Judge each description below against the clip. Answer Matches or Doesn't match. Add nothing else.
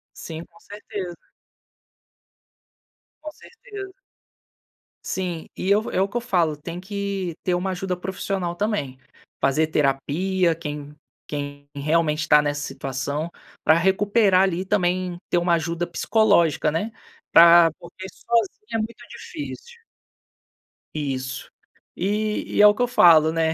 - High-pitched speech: Doesn't match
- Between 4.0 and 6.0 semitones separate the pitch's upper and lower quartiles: Matches